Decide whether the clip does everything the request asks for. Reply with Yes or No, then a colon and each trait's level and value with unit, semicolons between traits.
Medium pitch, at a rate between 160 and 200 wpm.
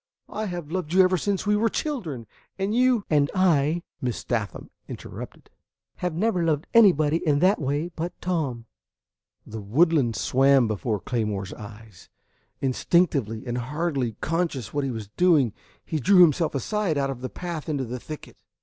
Yes: medium, 150 Hz; average, 165 wpm